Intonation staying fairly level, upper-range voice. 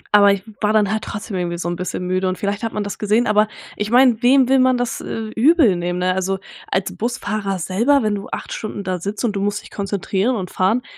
No: average, 3.1 semitones; high, 205 Hz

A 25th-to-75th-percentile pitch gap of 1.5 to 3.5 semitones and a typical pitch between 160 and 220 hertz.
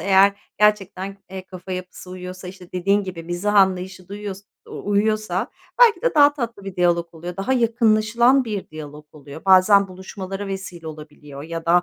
Yes: average, 2.7 semitones; high, 190 Hz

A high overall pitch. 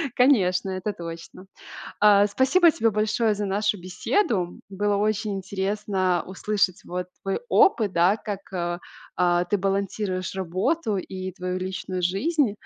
Yes: high, 195 Hz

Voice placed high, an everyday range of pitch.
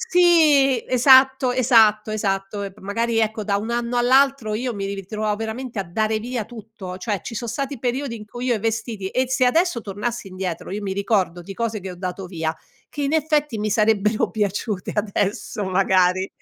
Yes: high, 220 Hz; average, 4.0 semitones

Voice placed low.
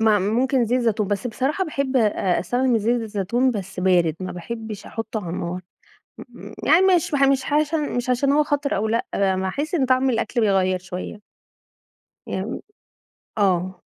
No: high, 225 Hz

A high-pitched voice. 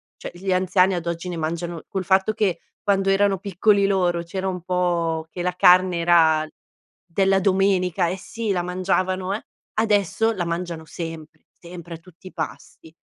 No: medium, 180 Hz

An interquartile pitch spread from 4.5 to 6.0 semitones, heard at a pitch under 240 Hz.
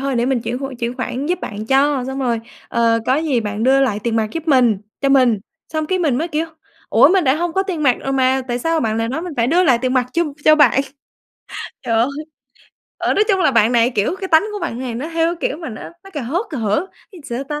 No: average, 5.1 semitones; very high, 270 Hz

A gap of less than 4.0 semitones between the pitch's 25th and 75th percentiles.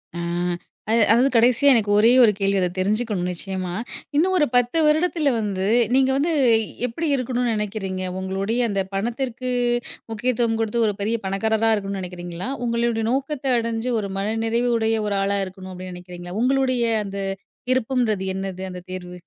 No: average, 4.3 semitones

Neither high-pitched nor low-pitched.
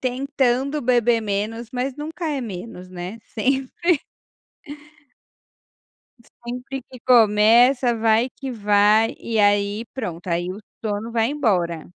No: high, 230 Hz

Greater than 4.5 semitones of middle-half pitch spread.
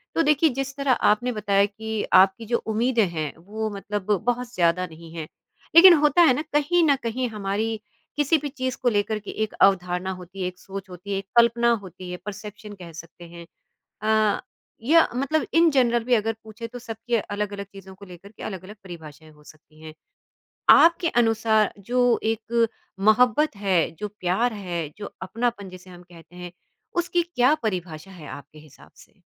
Yes: average, 5.0 semitones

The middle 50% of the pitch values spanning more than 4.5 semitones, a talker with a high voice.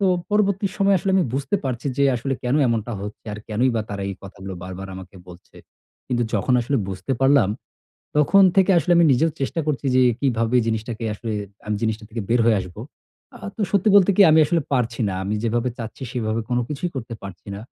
No: average, 5.1 semitones; low, 120 Hz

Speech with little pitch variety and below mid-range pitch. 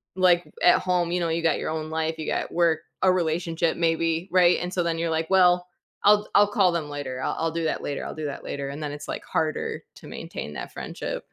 No: narrow, 2.1 semitones; medium, 165 Hz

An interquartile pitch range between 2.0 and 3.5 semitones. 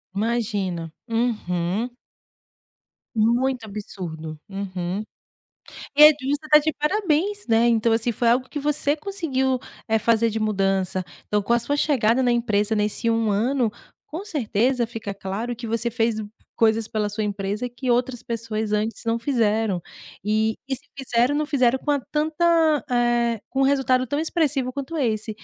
No: average, 4.0 semitones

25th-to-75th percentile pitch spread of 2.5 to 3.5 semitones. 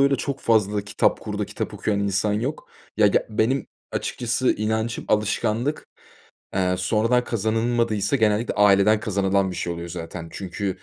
Yes: average, 2.8 semitones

